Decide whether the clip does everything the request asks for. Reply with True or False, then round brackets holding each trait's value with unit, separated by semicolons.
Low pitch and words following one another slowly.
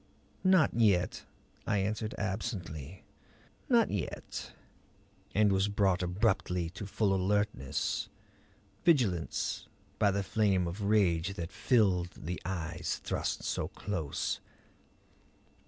True (95 Hz; 105 wpm)